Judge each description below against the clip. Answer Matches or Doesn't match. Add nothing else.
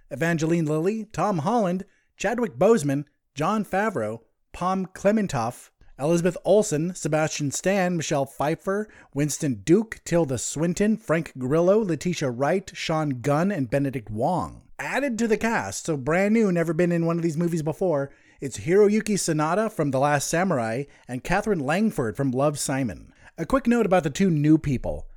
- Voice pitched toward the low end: Doesn't match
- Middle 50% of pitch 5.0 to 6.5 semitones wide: Matches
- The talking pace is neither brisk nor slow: Matches